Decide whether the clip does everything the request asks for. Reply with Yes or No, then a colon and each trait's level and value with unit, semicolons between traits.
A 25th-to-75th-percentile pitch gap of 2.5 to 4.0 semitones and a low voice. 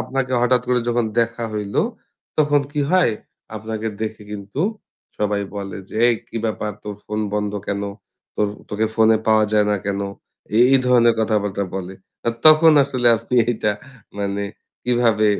Yes: average, 2.8 semitones; low, 110 Hz